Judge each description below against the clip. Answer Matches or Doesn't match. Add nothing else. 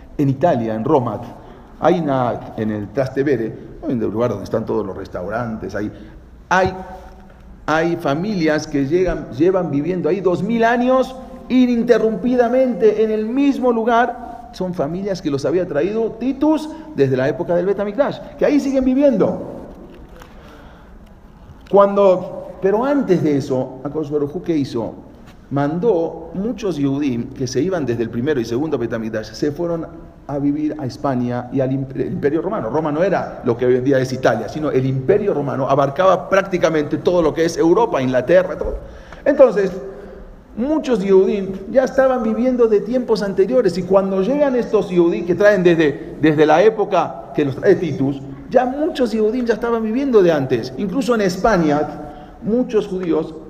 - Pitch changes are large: Matches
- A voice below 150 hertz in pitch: Doesn't match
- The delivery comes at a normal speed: Matches